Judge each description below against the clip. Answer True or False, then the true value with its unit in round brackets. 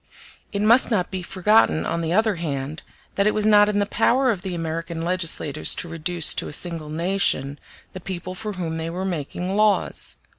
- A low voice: False (180 Hz)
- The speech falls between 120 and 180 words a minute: False (195 wpm)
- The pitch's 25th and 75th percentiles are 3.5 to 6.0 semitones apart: True (3.8 semitones)